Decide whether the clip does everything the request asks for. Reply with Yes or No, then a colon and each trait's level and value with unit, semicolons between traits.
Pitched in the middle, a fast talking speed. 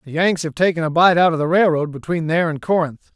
Yes: medium, 165 Hz; fast, 265 wpm